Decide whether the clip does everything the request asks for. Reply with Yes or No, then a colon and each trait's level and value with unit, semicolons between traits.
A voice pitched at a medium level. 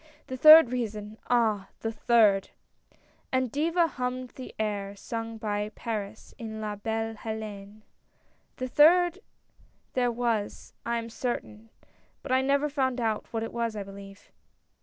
No: high, 225 Hz